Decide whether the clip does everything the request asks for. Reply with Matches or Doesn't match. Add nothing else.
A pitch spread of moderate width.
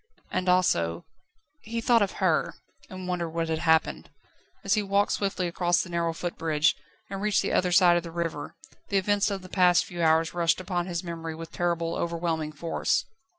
Doesn't match